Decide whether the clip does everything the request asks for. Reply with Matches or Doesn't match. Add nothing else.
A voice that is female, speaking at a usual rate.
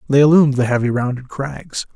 Doesn't match